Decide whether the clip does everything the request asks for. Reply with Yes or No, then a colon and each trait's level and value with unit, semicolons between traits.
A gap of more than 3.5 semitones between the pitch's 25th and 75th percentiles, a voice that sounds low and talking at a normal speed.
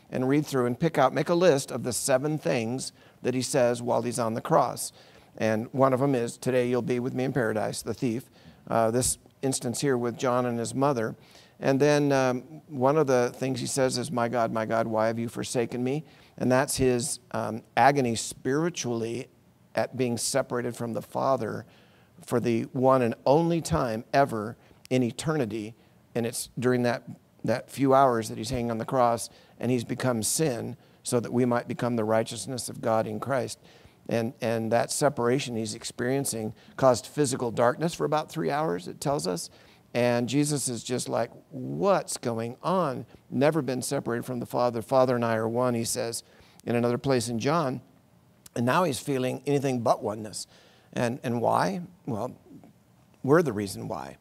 No: narrow, 2.6 semitones; low, 125 Hz; average, 185 wpm